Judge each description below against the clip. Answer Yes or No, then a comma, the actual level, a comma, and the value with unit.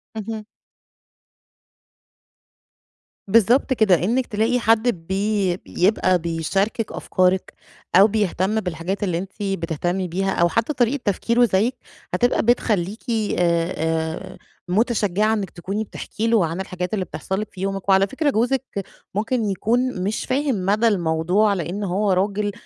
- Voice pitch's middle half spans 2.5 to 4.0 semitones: Yes, average, 3.5 semitones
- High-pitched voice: Yes, high, 200 Hz